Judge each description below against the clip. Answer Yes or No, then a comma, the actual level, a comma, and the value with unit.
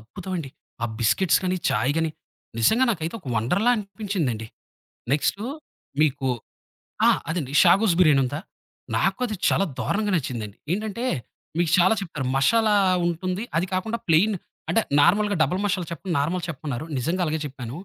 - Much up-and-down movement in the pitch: Yes, wide, 6.1 semitones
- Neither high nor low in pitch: Yes, medium, 175 Hz